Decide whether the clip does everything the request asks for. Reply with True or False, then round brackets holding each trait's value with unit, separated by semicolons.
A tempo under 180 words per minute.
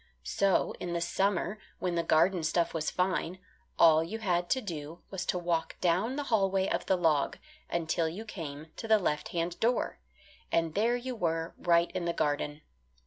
False (185 wpm)